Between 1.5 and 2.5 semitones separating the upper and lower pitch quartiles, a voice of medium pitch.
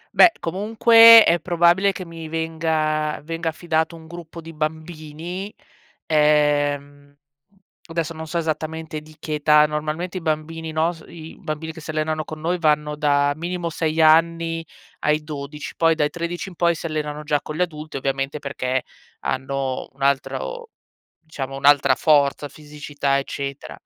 Yes: narrow, 1.9 semitones; medium, 155 Hz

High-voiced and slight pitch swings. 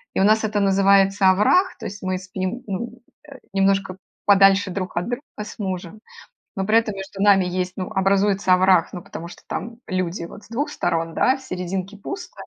Yes: high, 195 Hz; narrow, 2.3 semitones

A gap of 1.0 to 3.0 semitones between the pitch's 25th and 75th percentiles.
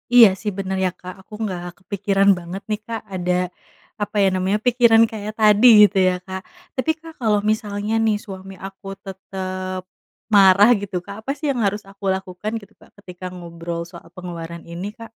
Yes: narrow, 2.4 semitones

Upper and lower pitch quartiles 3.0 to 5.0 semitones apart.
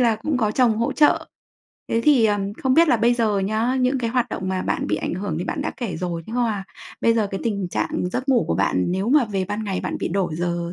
Yes: average, 4.5 semitones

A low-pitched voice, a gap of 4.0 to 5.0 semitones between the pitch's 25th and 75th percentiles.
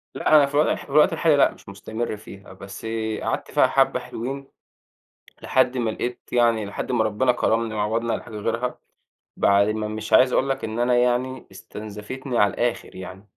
No: low, 115 Hz; average, 3.4 semitones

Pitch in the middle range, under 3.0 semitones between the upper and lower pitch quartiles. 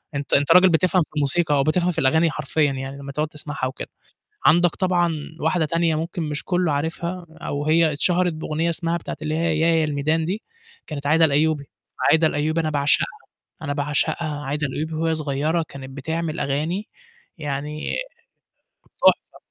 Yes: medium, 155 Hz; narrow, 2.5 semitones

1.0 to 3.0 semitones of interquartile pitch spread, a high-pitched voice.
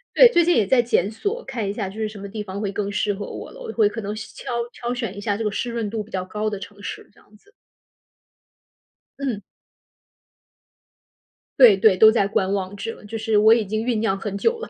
Yes: narrow, 2.4 semitones; high, 215 Hz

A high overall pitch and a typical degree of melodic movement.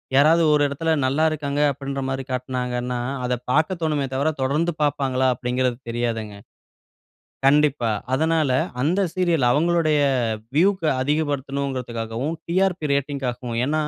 No: medium, 140 Hz; average, 3.5 semitones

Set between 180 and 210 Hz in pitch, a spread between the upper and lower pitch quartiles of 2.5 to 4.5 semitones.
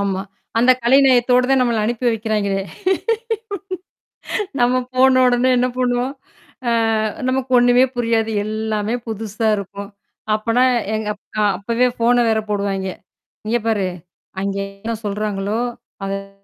No: high, 225 Hz; average, 3.3 semitones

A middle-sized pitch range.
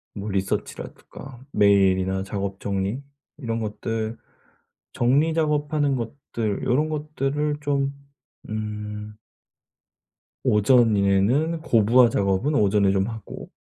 No: wide, 5.8 semitones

